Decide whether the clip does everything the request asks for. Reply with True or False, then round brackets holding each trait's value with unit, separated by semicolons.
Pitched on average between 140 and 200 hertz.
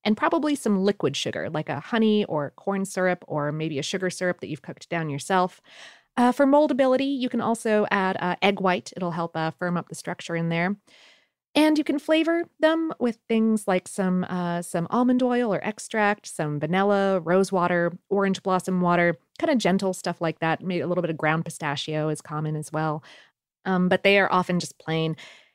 True (185 Hz)